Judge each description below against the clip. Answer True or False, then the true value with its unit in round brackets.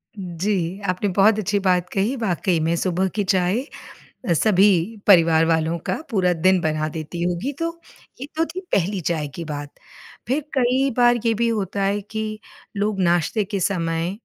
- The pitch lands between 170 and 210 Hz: True (190 Hz)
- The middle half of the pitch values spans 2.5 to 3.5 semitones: False (4.0 semitones)